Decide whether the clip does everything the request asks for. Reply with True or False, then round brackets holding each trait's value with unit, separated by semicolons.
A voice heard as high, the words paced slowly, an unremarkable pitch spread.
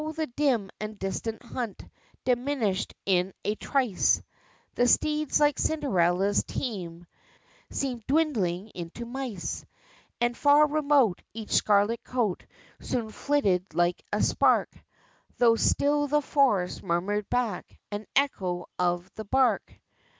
False (230 Hz; 120 wpm; 6.2 semitones)